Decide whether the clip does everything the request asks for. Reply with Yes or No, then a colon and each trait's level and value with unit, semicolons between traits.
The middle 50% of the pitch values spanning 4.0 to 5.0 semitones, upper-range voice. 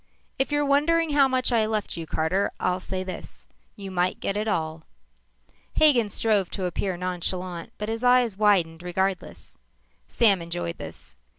Yes: average, 4.7 semitones; high, 195 Hz